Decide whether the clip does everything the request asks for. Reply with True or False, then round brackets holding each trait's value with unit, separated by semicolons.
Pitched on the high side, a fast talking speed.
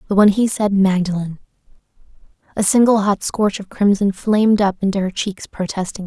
False (200 Hz; 170 wpm)